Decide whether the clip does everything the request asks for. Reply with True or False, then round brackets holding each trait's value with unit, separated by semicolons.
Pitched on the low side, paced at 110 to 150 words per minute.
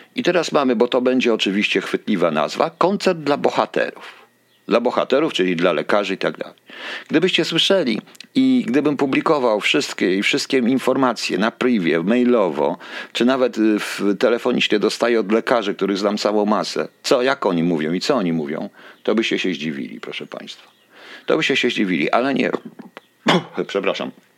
False (120 Hz; 160 wpm)